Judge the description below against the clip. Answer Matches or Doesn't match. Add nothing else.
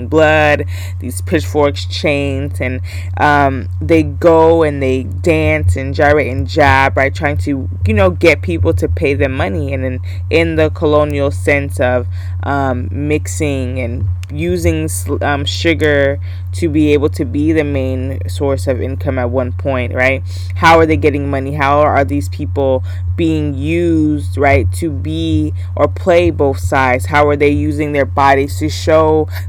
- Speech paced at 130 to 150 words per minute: Doesn't match